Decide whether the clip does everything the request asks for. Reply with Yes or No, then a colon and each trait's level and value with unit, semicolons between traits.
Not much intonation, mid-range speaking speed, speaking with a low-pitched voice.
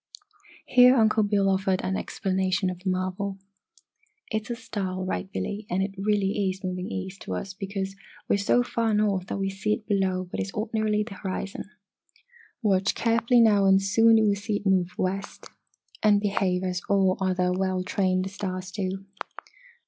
No: narrow, 2.0 semitones; average, 180 wpm; high, 195 Hz